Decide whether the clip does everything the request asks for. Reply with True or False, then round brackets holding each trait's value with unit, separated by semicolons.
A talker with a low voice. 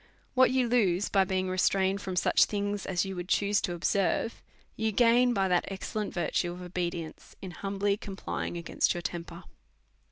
False (195 Hz)